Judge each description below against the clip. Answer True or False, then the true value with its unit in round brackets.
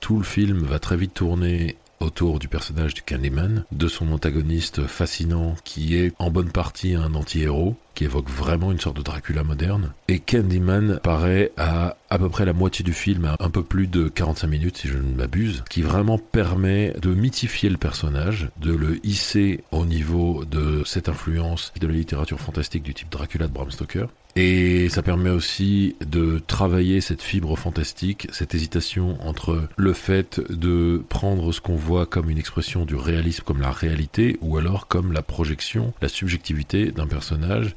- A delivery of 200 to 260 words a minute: False (180 wpm)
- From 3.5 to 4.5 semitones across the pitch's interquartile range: False (3.0 semitones)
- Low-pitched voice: True (85 Hz)